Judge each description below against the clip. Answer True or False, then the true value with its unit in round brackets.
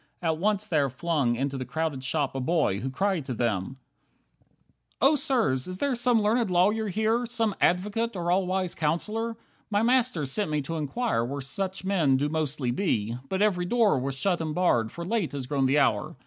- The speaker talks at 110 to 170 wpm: False (200 wpm)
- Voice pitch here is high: False (170 Hz)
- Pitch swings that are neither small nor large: False (7.5 semitones)